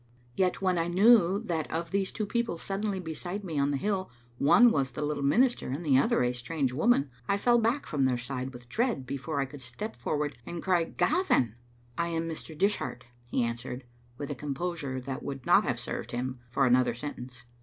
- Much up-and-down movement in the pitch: Yes, wide, 6.5 semitones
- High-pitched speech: No, medium, 150 Hz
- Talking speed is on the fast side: Yes, fast, 210 wpm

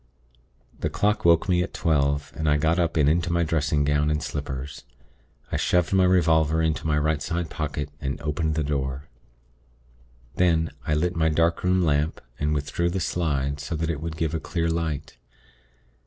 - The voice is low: Yes, very low, 80 Hz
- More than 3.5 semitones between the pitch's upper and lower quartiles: No, narrow, 2.4 semitones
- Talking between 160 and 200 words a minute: Yes, average, 180 wpm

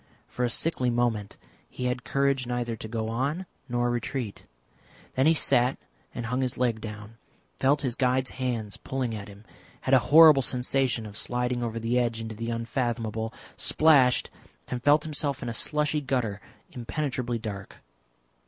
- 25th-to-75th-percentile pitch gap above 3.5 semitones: No, narrow, 2.6 semitones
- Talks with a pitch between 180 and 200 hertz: No, low, 125 Hz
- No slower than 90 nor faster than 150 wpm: No, average, 160 wpm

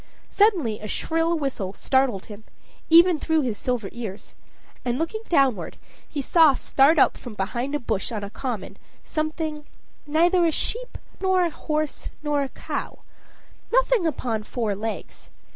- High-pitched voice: Yes, very high, 285 Hz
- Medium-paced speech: Yes, average, 150 wpm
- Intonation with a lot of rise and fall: Yes, wide, 6.3 semitones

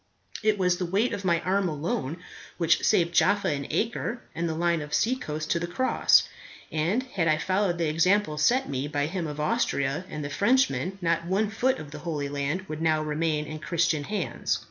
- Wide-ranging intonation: No, average, 4.2 semitones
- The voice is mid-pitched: Yes, medium, 170 Hz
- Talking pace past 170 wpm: Yes, average, 200 wpm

